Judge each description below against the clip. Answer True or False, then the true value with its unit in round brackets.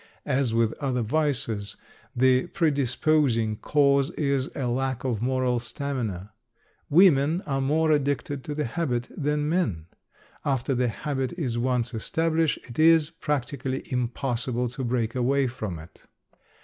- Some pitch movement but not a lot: True (3.5 semitones)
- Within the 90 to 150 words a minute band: True (135 wpm)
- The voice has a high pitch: False (130 Hz)